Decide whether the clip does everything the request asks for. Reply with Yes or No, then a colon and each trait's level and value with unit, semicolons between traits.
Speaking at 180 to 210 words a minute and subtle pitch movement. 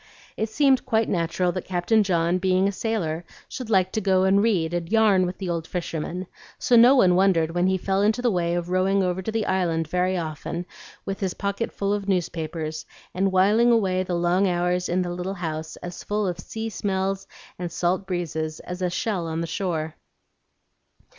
Yes: average, 200 wpm; narrow, 2.3 semitones